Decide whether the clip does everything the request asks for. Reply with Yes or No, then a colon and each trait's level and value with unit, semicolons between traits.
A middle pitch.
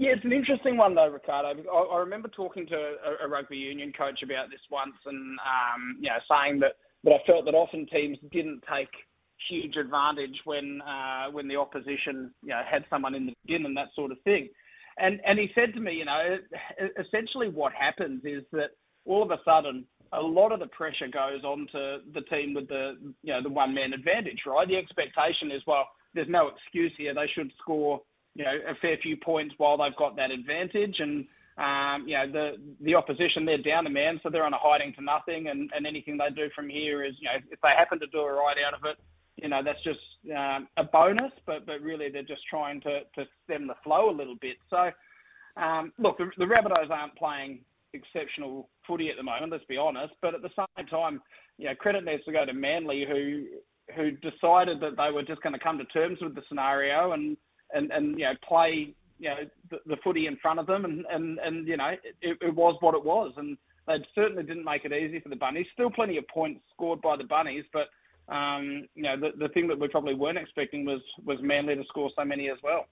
Yes: medium, 150 Hz